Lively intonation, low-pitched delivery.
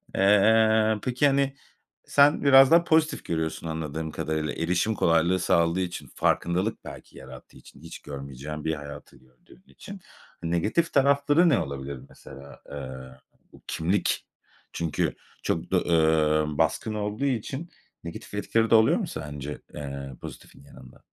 Yes: wide, 7.3 semitones; very low, 85 Hz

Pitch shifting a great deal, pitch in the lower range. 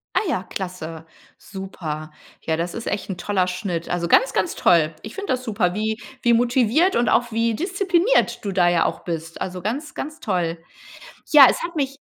No: wide, 6.5 semitones; high, 205 Hz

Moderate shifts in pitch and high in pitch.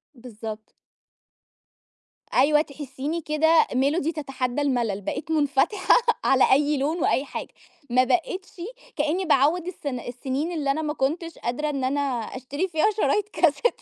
Yes: average, 3.5 semitones; very high, 290 Hz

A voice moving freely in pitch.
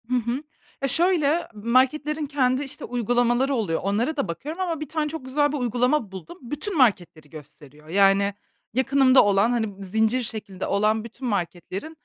Yes: wide, 6.1 semitones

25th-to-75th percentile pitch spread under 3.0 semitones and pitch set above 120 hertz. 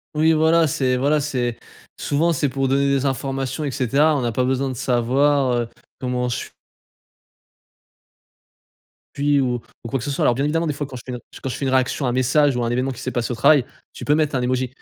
Yes: narrow, 2.5 semitones; low, 135 Hz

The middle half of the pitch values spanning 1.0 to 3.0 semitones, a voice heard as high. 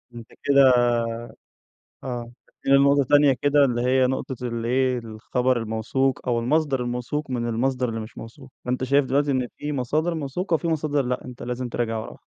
No: average, 2.7 semitones; low, 130 Hz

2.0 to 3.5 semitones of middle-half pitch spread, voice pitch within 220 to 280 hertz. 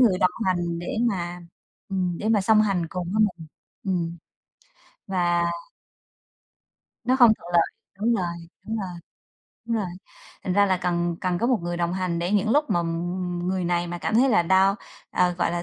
No: average, 3.1 semitones; medium, 185 Hz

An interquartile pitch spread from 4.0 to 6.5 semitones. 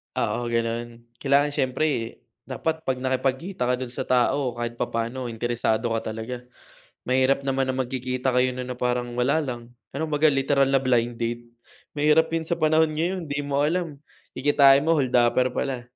No: average, 2.9 semitones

